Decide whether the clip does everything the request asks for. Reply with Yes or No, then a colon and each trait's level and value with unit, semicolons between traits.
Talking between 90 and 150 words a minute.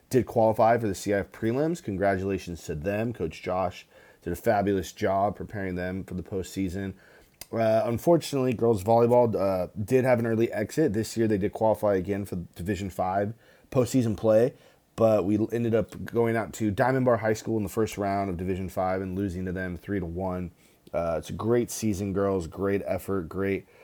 No: average, 190 wpm